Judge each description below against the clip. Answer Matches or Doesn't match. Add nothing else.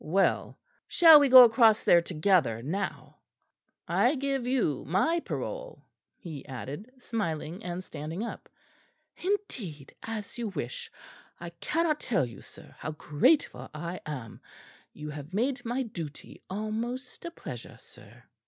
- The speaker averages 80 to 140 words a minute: Matches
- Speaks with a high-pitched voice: Matches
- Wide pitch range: Matches